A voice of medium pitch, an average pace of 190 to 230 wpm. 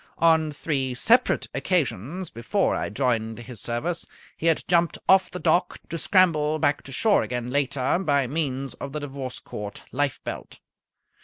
No: medium, 145 Hz; average, 155 wpm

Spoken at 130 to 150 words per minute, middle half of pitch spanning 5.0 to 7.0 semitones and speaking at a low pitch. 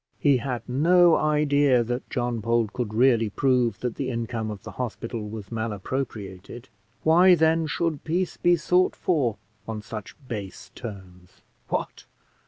Yes: average, 145 wpm; average, 5.3 semitones; low, 120 Hz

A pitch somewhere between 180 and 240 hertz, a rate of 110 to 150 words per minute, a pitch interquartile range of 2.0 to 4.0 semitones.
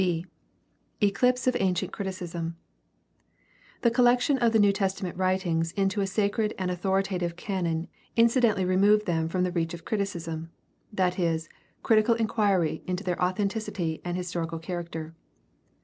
Yes: medium, 185 Hz; average, 145 wpm; average, 3.4 semitones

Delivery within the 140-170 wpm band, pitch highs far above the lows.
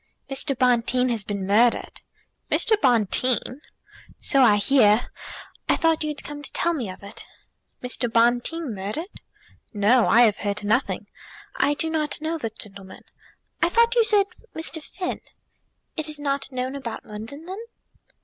Yes: average, 155 wpm; wide, 5.8 semitones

